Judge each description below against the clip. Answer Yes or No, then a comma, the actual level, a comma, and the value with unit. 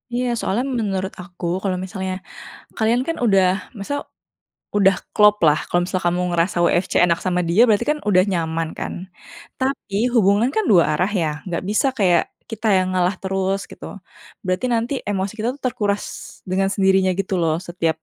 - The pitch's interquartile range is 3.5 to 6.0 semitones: No, average, 2.7 semitones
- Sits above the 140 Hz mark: Yes, high, 190 Hz